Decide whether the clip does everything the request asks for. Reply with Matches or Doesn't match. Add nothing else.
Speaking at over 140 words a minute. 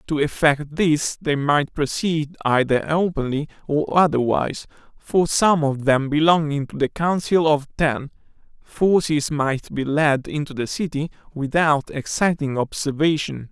Doesn't match